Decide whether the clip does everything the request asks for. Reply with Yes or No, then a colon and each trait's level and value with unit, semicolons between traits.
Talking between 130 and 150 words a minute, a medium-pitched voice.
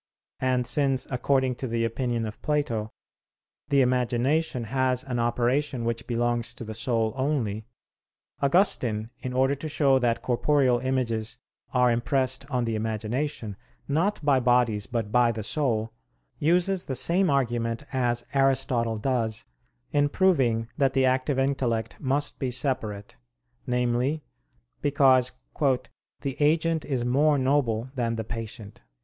No: slow, 135 wpm; low, 125 Hz